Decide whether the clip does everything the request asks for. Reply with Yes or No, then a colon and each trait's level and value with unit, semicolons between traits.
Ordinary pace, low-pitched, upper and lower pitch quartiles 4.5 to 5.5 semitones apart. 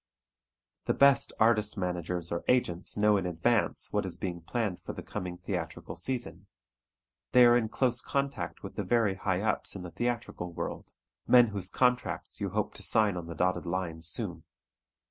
Yes: average, 175 wpm; low, 100 Hz; average, 5.2 semitones